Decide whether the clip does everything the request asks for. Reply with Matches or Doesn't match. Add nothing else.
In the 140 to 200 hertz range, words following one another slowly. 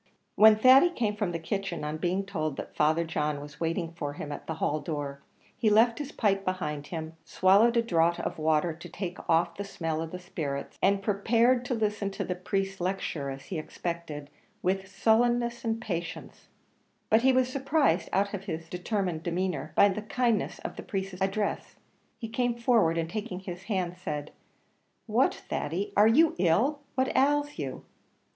Doesn't match